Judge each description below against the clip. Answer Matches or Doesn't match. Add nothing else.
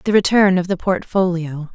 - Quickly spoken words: Doesn't match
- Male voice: Doesn't match